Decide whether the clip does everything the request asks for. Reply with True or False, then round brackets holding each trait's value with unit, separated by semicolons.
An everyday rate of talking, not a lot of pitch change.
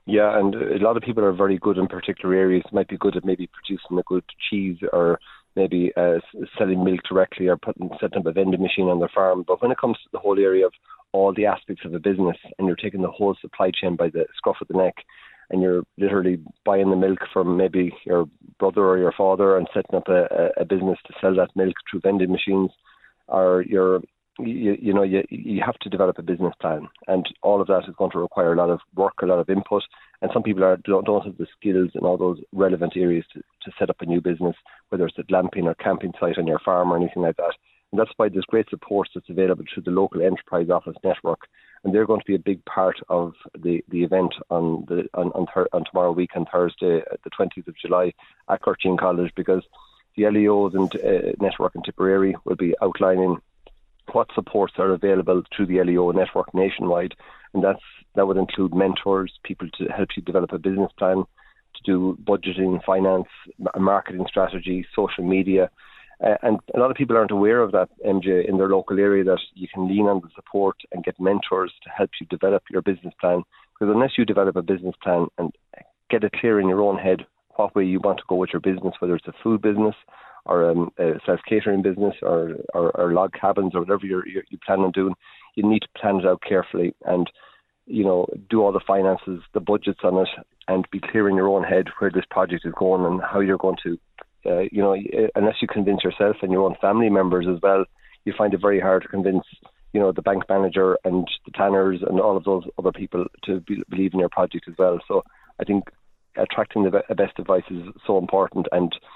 False (225 wpm; 1.4 semitones)